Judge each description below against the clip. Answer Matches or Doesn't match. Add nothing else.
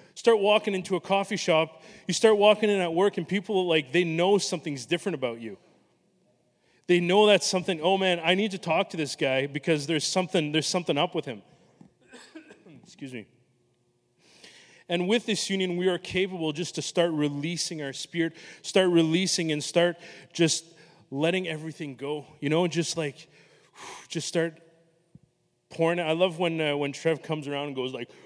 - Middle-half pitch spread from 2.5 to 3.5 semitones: Matches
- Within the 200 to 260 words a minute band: Doesn't match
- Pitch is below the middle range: Doesn't match